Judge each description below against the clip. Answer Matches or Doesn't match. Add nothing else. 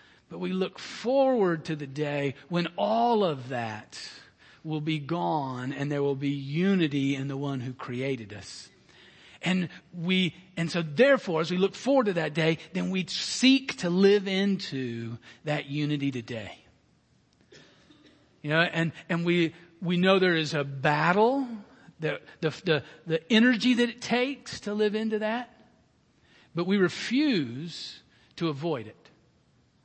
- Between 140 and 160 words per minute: Matches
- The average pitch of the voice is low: Doesn't match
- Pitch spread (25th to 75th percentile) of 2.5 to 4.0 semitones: Doesn't match